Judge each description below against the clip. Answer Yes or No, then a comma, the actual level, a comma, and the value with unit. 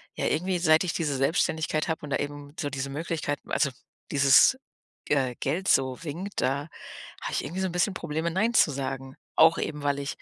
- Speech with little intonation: No, average, 3.4 semitones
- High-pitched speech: No, medium, 150 Hz